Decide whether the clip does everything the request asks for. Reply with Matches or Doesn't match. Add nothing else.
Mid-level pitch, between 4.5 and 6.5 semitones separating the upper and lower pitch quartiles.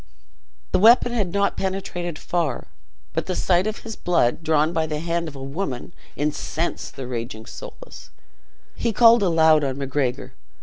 Matches